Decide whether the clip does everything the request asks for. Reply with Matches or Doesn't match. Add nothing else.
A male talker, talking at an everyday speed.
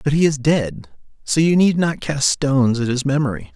Doesn't match